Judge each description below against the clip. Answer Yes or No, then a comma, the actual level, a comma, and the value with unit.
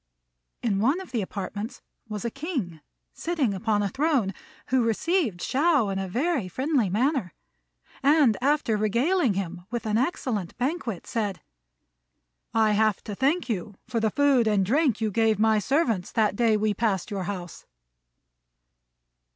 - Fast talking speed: No, average, 150 wpm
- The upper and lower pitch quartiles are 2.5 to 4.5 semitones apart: No, average, 5.2 semitones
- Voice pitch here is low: No, high, 225 Hz